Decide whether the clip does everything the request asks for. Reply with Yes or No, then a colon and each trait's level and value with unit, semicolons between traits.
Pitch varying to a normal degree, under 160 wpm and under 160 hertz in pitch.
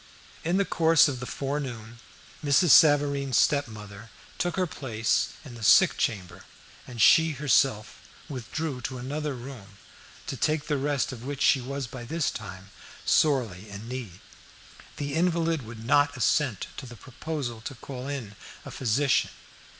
Yes: average, 4.3 semitones; average, 150 wpm; low, 135 Hz